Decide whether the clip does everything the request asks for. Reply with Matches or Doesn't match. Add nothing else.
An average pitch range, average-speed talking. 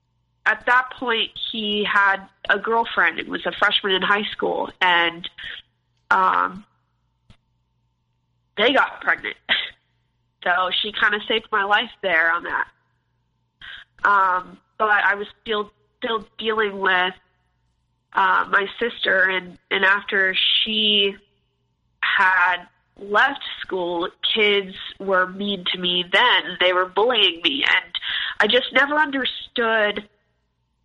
Doesn't match